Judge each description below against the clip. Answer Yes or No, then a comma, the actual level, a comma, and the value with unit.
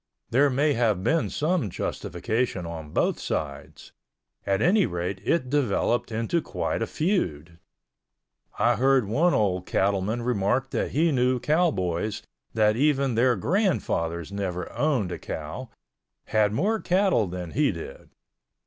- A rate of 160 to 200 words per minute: No, slow, 135 wpm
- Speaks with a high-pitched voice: No, low, 115 Hz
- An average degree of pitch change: No, wide, 7.9 semitones